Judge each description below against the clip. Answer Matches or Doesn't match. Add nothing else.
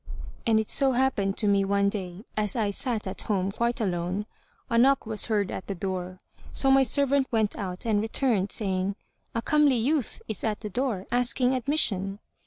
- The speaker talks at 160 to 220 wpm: Matches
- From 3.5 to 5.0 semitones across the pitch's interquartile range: Matches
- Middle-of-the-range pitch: Doesn't match